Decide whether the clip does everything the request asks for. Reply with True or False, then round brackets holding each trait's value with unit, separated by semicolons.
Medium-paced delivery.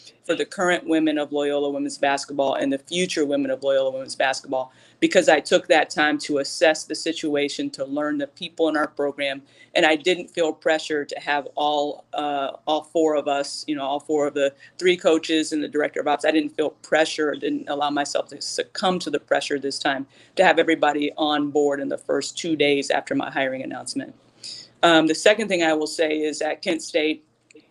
False (210 wpm)